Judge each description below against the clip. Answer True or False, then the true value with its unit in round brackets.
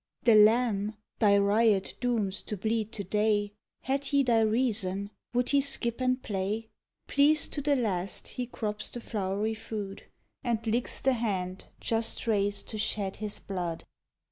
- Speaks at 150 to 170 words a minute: True (155 wpm)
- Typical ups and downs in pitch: True (3.0 semitones)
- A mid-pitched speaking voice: False (220 Hz)